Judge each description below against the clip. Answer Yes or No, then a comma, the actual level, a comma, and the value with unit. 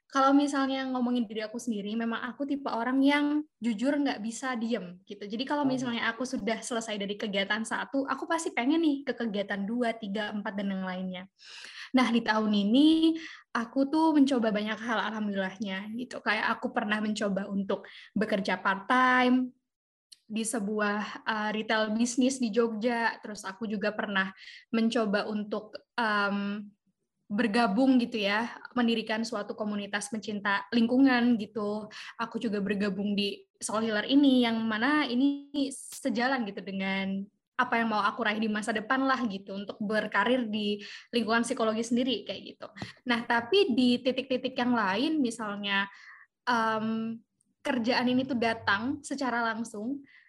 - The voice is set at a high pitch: Yes, high, 230 Hz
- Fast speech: Yes, fast, 150 wpm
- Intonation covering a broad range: No, average, 3.2 semitones